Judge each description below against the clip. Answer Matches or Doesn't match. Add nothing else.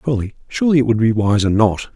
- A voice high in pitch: Doesn't match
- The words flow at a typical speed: Matches